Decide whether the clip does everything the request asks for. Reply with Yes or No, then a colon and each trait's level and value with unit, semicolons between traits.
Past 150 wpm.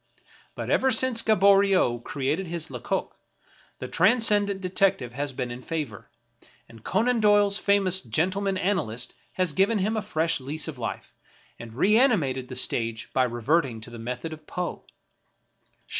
No: average, 145 wpm